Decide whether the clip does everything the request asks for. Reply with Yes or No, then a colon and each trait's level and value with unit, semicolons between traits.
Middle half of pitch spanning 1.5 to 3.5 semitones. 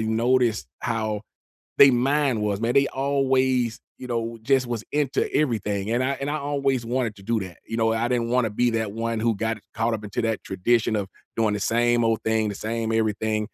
Yes: narrow, 2.4 semitones